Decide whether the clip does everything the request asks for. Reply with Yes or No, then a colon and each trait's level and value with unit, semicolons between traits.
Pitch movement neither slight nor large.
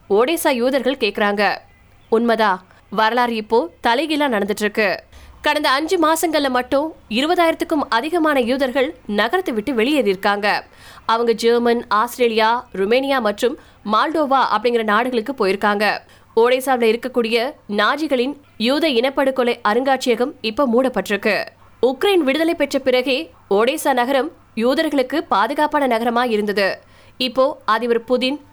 Yes: average, 4.3 semitones